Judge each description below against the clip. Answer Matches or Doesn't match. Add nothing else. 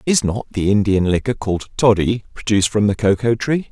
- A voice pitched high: Doesn't match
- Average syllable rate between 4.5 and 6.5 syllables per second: Matches